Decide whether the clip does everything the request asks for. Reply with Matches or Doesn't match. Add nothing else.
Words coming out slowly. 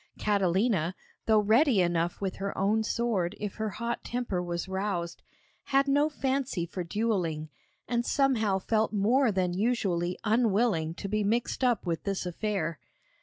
Doesn't match